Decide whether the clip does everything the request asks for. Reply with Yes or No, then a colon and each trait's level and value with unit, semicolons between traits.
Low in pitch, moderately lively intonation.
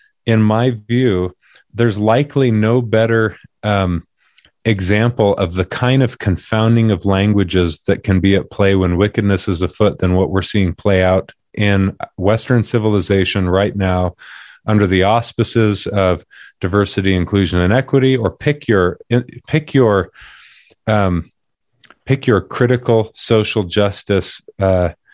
Yes: low, 105 Hz; average, 3.4 semitones